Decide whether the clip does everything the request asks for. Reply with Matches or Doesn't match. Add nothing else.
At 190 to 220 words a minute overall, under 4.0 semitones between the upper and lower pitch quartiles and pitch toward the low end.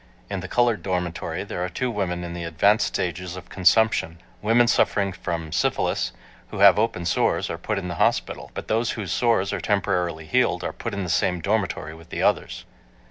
Matches